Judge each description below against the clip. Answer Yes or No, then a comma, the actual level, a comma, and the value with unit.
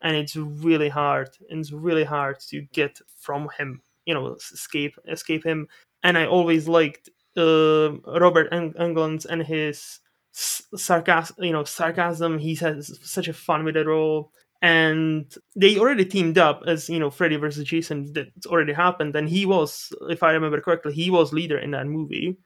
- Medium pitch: Yes, medium, 160 Hz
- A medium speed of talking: Yes, average, 170 wpm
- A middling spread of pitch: No, narrow, 2.0 semitones